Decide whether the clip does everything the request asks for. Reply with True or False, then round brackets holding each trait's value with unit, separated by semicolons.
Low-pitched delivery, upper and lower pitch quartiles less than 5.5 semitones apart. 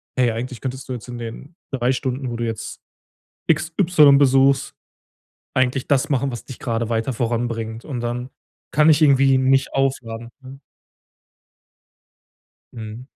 True (130 Hz; 2.5 semitones)